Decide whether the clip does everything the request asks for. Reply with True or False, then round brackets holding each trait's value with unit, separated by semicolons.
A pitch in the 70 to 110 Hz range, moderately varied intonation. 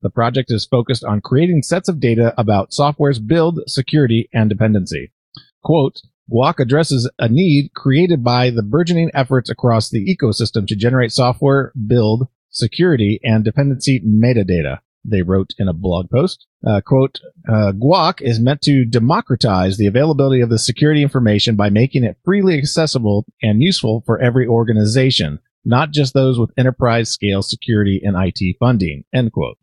False (120 Hz; 4.2 semitones)